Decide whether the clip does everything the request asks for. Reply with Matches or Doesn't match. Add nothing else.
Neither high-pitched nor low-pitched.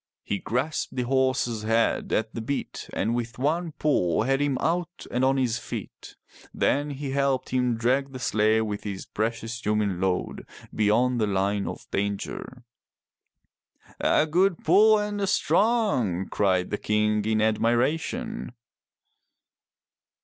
Doesn't match